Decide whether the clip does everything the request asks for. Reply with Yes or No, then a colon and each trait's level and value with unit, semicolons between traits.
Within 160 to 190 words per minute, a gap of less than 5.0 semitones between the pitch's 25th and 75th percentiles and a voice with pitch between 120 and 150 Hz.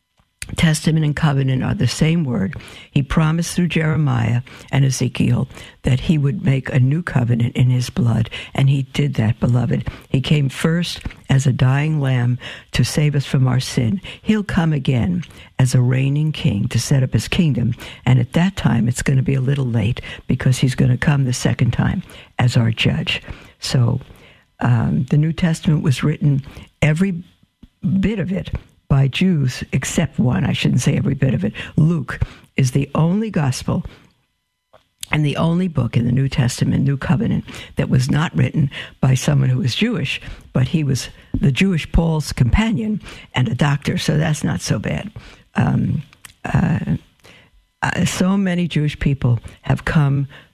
Yes: average, 170 wpm; average, 4.1 semitones; medium, 140 Hz